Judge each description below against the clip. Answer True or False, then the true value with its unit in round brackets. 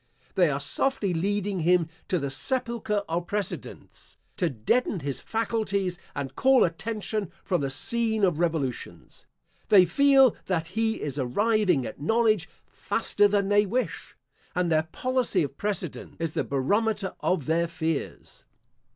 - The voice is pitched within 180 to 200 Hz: True (185 Hz)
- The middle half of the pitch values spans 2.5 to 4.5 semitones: False (5.2 semitones)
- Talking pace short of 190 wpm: True (140 wpm)